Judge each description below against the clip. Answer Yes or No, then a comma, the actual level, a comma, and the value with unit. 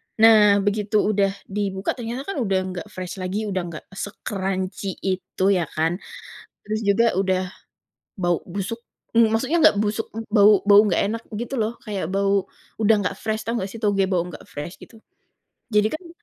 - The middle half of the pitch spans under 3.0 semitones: Yes, narrow, 2.6 semitones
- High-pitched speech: Yes, high, 200 Hz